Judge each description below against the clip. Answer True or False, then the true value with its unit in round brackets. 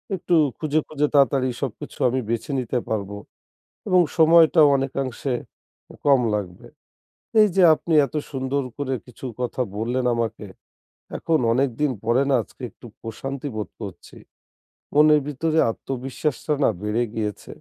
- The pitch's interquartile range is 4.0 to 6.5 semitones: True (4.3 semitones)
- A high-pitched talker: False (135 Hz)